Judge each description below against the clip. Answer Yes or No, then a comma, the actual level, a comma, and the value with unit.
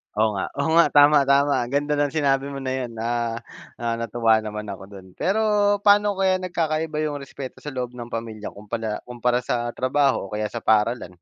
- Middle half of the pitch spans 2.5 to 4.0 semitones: No, average, 4.5 semitones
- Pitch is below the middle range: Yes, low, 125 Hz